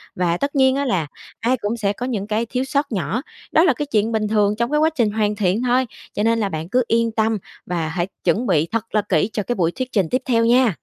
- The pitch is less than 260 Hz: Yes, high, 220 Hz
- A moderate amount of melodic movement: Yes, average, 4.0 semitones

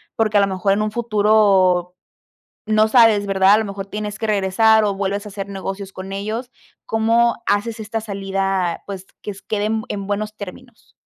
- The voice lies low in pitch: No, high, 205 Hz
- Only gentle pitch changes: Yes, narrow, 1.9 semitones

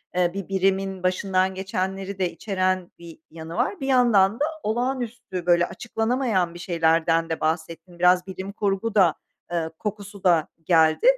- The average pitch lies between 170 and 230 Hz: Yes, high, 190 Hz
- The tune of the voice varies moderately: Yes, average, 3.1 semitones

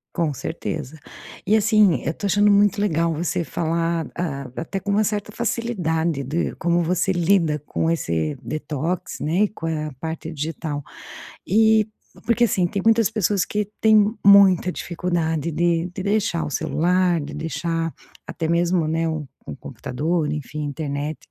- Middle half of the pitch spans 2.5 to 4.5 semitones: Yes, average, 4.1 semitones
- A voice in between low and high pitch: Yes, medium, 170 Hz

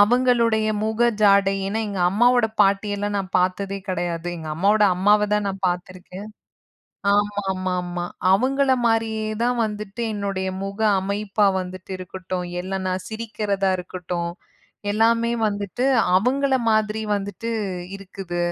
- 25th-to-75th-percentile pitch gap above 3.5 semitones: No, average, 2.7 semitones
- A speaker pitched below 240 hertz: Yes, high, 200 Hz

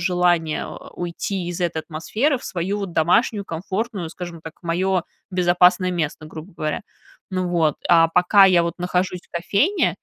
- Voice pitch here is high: No, medium, 175 Hz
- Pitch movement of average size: No, narrow, 2.3 semitones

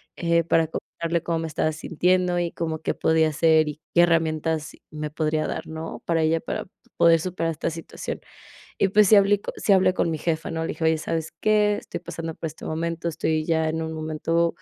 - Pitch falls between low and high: Yes, medium, 165 Hz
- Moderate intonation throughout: No, narrow, 1.1 semitones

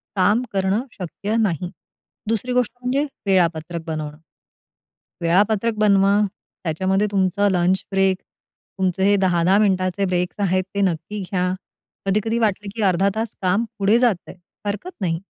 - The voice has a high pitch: Yes, high, 195 Hz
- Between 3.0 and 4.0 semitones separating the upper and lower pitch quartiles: No, narrow, 2.5 semitones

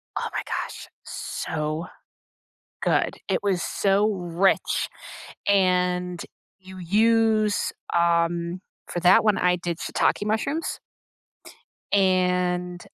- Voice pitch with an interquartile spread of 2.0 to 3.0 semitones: Yes, narrow, 2.5 semitones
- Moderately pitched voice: Yes, medium, 180 Hz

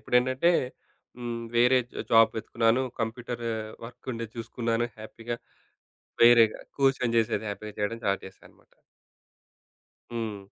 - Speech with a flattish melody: Yes, narrow, 1.3 semitones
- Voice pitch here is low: Yes, low, 115 Hz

